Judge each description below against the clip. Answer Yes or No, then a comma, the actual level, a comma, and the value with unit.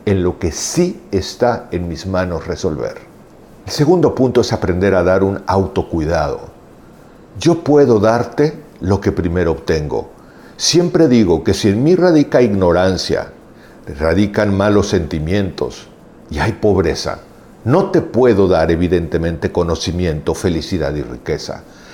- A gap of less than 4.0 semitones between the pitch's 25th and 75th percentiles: No, average, 4.8 semitones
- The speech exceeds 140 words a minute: No, average, 130 wpm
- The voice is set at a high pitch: No, very low, 95 Hz